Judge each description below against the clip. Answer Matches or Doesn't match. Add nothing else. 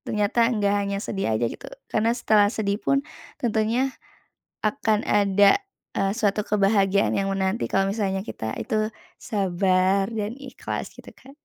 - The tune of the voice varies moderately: Doesn't match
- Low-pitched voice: Doesn't match